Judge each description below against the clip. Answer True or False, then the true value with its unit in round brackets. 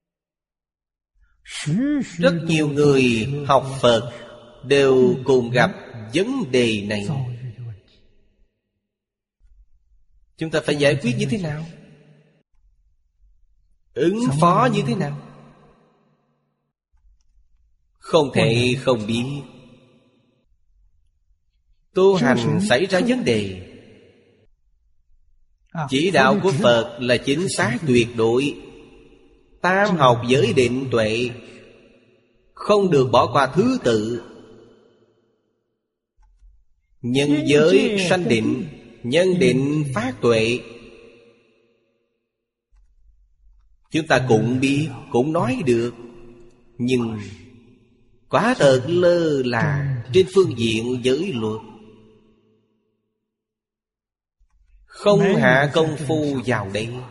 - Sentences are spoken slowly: True (90 wpm)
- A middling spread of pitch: True (5.0 semitones)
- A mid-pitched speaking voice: False (120 Hz)